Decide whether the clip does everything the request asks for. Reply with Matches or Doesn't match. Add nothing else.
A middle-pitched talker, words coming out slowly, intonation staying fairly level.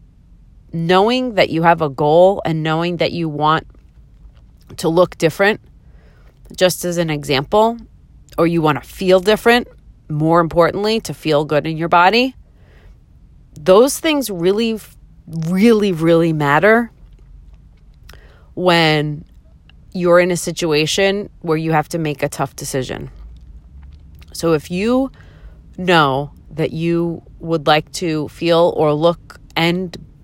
Doesn't match